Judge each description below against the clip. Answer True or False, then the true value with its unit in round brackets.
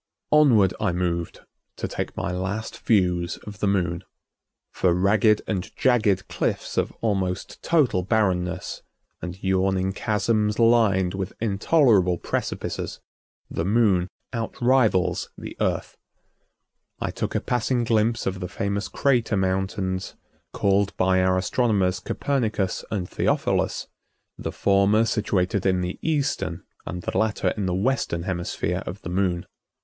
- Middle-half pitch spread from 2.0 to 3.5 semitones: True (3.2 semitones)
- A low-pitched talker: True (95 Hz)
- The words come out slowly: True (130 wpm)